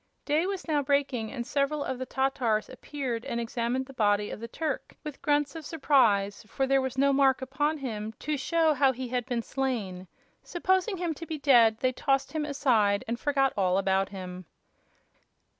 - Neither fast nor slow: Yes, average, 190 wpm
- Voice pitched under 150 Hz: No, very high, 265 Hz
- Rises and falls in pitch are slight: No, average, 4.2 semitones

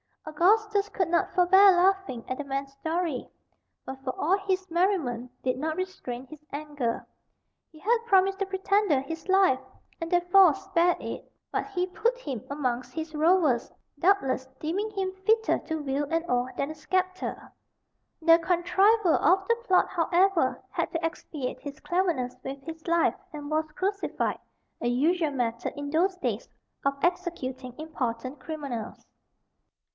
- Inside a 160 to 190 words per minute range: No, average, 150 wpm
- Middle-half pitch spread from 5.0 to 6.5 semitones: Yes, wide, 5.4 semitones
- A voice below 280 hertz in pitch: No, very high, 330 Hz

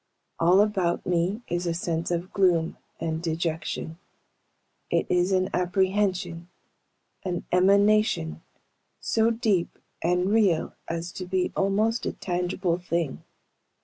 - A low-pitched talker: No, medium, 180 Hz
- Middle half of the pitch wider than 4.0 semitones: No, narrow, 2.4 semitones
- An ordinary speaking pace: No, slow, 115 wpm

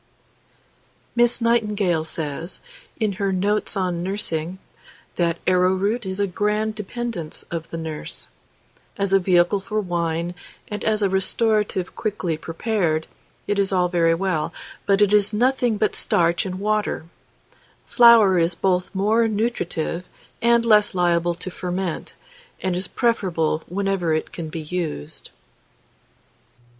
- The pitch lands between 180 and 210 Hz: Yes, high, 190 Hz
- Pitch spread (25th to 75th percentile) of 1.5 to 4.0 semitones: Yes, average, 3.6 semitones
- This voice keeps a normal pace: No, slow, 130 wpm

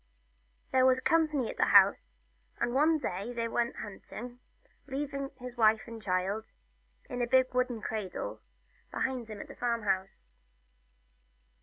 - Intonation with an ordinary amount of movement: Yes, average, 3.1 semitones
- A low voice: No, high, 240 Hz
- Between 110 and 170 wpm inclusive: Yes, average, 150 wpm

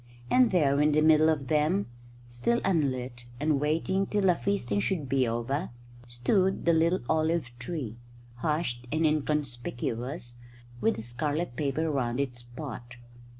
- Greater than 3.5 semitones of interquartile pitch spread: Yes, average, 5.1 semitones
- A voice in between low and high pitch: Yes, medium, 150 Hz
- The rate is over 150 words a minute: No, average, 145 wpm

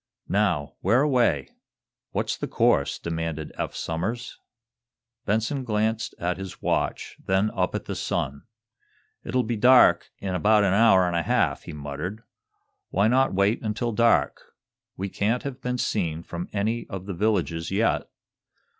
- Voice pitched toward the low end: Yes, low, 100 Hz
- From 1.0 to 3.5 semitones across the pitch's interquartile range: No, average, 4.6 semitones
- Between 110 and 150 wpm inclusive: Yes, average, 145 wpm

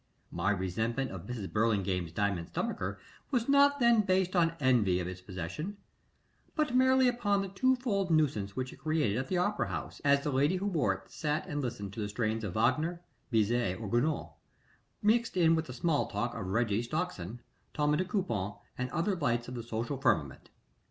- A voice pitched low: Yes, low, 130 Hz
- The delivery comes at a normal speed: Yes, average, 185 wpm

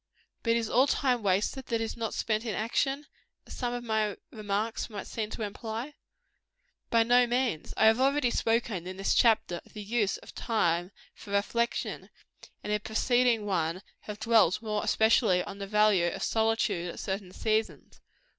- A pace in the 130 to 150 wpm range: No, average, 175 wpm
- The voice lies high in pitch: Yes, high, 220 Hz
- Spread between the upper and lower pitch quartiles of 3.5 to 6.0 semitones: No, narrow, 2.6 semitones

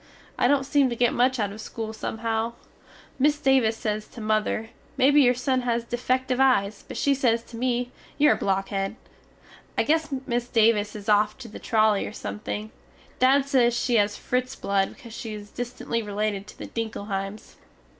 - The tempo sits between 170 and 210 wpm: Yes, average, 180 wpm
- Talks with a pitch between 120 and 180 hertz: No, high, 230 Hz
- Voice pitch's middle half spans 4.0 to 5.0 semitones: No, average, 3.3 semitones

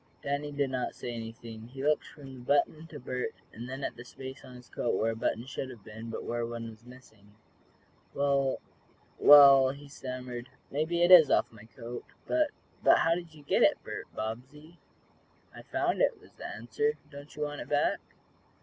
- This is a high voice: No, low, 130 Hz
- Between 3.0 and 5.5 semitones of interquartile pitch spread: Yes, average, 3.7 semitones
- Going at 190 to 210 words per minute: Yes, average, 195 wpm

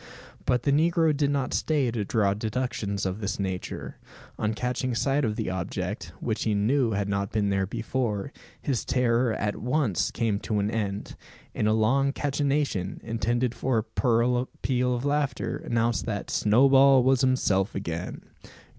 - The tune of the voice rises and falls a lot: No, average, 4.3 semitones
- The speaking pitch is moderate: No, low, 115 Hz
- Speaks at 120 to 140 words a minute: No, average, 160 wpm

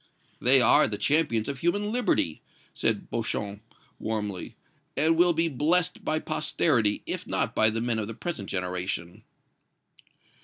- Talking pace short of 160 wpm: Yes, average, 145 wpm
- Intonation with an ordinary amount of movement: No, wide, 7.8 semitones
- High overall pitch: No, low, 120 Hz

